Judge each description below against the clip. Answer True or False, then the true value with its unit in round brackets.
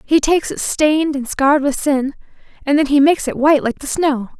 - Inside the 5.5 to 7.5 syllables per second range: True (5.9 syllables/s)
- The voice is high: True (290 Hz)